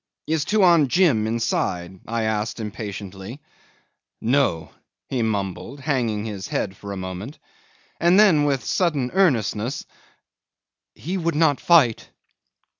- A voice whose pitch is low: Yes, low, 120 Hz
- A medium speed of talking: No, slow, 115 wpm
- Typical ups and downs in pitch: No, wide, 6.8 semitones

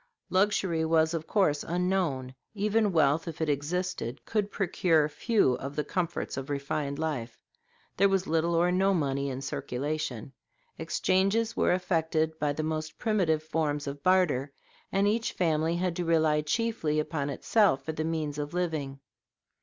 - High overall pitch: No, medium, 160 Hz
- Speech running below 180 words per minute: Yes, average, 155 wpm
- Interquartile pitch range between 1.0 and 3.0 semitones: No, average, 3.9 semitones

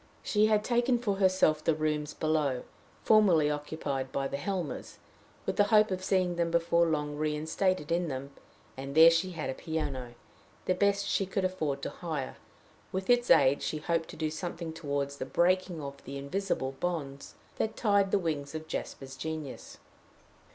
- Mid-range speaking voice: Yes, medium, 160 Hz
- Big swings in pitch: No, average, 4.4 semitones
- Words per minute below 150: No, average, 170 wpm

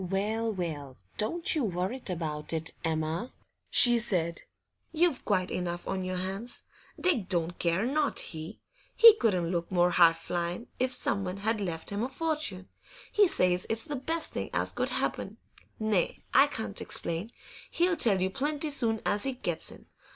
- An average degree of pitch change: No, wide, 6.4 semitones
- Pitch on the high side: Yes, high, 195 Hz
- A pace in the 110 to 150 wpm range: No, average, 165 wpm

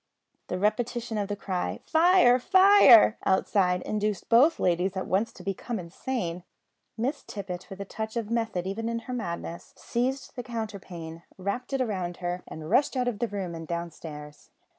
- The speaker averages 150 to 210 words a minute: Yes, average, 170 wpm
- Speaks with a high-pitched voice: Yes, high, 210 Hz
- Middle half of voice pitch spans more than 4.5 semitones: Yes, average, 5.0 semitones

